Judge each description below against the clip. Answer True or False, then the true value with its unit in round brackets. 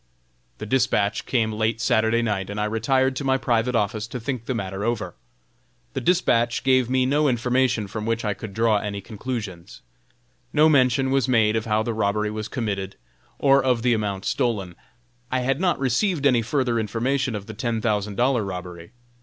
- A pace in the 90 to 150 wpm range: False (185 wpm)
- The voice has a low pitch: True (115 Hz)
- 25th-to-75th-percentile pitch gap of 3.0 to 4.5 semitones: True (3.4 semitones)